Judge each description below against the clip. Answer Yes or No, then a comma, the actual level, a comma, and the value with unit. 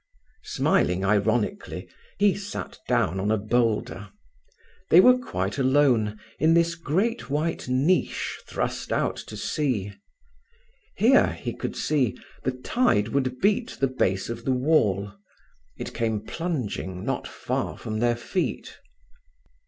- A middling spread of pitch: No, wide, 7.6 semitones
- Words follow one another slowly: Yes, slow, 130 wpm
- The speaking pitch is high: No, low, 125 Hz